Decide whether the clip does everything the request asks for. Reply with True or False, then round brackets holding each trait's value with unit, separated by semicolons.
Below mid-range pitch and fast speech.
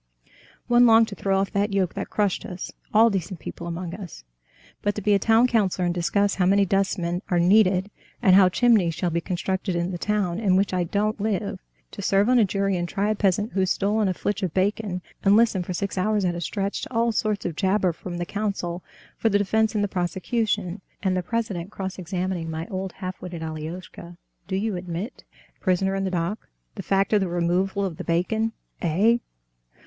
False (195 Hz; 210 wpm)